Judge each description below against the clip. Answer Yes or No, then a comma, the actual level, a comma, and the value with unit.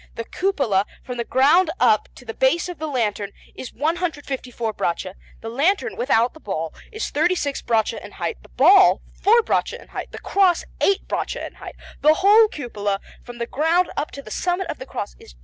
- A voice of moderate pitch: No, very high, 275 Hz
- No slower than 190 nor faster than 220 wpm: Yes, fast, 205 wpm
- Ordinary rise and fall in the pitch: No, wide, 7.9 semitones